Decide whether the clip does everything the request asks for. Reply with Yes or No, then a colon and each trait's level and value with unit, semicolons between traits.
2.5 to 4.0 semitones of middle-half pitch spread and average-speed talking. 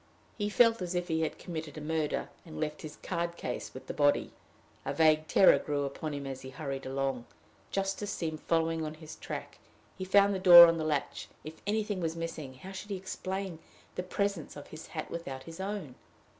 No: average, 3.7 semitones; fast, 210 wpm